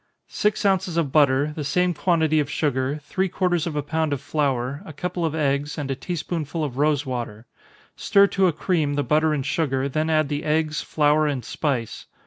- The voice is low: No, medium, 150 Hz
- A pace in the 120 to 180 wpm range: No, fast, 205 wpm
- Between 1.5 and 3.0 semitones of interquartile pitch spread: Yes, narrow, 2.6 semitones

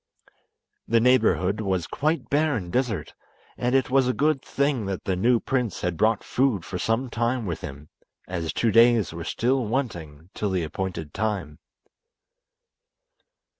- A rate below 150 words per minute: No, average, 155 wpm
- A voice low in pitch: Yes, low, 110 Hz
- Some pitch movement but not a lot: No, wide, 5.9 semitones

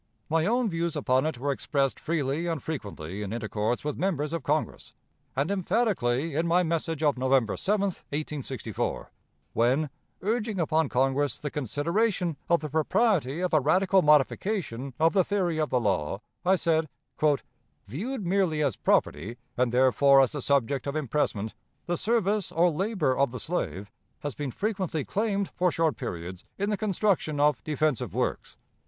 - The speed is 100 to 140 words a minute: No, average, 160 wpm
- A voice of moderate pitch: Yes, medium, 155 Hz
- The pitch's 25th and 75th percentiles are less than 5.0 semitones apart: No, wide, 5.5 semitones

